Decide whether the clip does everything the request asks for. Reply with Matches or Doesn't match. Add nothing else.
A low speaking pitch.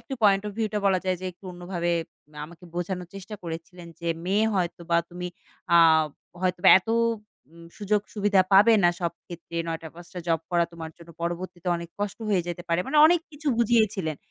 Doesn't match